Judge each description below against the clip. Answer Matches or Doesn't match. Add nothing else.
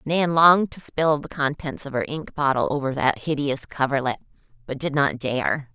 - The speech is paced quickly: Doesn't match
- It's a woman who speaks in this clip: Matches